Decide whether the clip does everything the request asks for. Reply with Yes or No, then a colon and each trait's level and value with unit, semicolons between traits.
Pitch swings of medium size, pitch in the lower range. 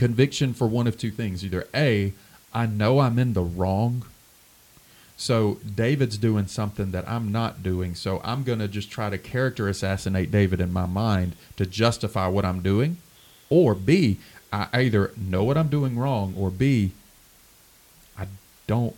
Yes: average, 3.8 semitones; low, 105 Hz